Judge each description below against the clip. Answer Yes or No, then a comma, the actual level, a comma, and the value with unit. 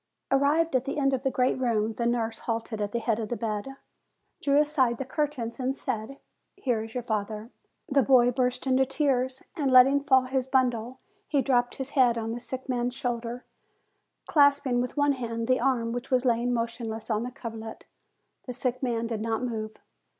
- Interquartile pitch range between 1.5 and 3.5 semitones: Yes, narrow, 2.6 semitones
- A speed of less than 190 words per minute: No, average, 200 wpm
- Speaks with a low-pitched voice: No, high, 245 Hz